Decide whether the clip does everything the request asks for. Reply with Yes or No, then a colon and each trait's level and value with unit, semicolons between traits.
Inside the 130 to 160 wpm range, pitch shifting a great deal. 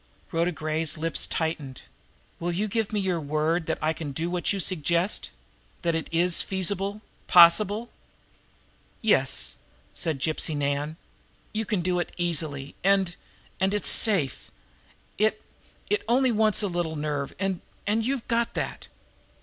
No: average, 145 wpm; average, 4.4 semitones